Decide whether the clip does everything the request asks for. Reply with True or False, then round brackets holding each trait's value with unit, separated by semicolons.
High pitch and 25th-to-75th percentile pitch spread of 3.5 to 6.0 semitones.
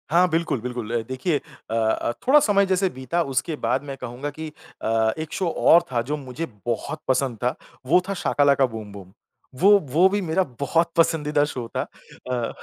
False (145 Hz; 5.4 semitones)